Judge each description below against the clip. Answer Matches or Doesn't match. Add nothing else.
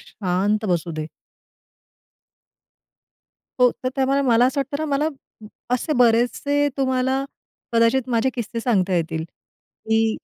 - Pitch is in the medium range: Doesn't match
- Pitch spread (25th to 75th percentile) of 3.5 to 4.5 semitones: Matches